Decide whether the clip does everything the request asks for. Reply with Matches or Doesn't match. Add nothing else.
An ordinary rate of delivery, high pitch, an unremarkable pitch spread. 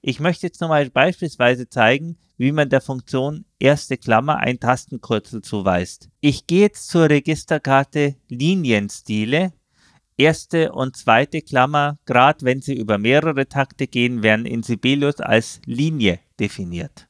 Doesn't match